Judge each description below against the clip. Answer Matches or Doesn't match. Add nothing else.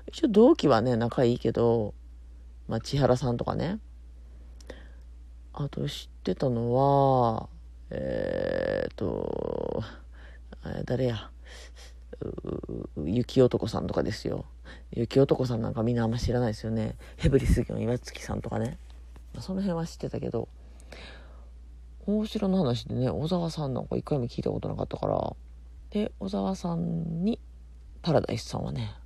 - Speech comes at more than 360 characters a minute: Doesn't match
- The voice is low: Matches